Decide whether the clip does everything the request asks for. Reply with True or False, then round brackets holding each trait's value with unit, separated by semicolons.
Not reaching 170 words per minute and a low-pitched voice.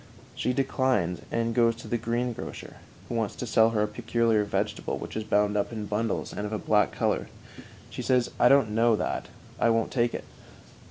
False (200 wpm; 115 Hz)